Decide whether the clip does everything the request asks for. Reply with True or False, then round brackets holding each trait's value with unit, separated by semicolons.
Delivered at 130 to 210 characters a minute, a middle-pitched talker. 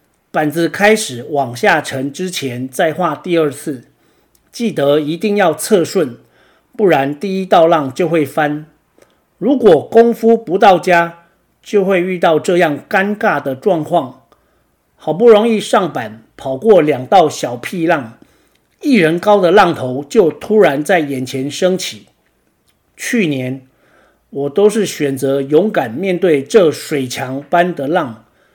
True (195 characters per minute; 165 Hz)